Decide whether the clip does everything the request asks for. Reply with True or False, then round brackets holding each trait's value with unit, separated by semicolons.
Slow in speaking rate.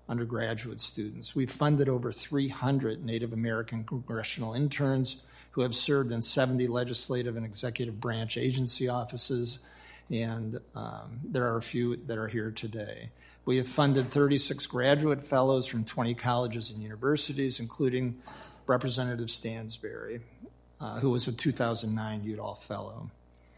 True (130 wpm)